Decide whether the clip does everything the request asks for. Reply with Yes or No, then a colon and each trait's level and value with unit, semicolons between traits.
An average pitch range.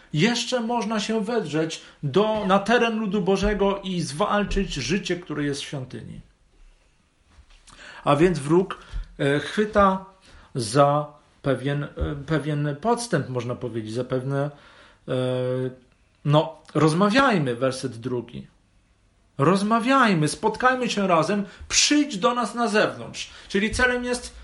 No: wide, 7.8 semitones